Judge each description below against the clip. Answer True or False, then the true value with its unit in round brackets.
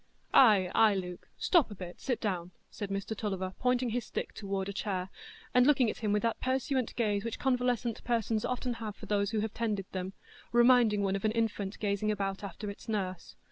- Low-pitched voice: False (210 Hz)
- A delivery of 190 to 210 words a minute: True (205 wpm)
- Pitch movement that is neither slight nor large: True (3.3 semitones)